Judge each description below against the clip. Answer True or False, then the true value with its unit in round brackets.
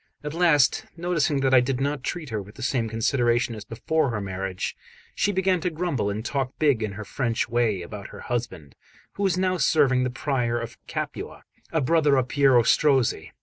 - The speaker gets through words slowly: False (195 wpm)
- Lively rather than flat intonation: False (4.8 semitones)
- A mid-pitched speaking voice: False (130 Hz)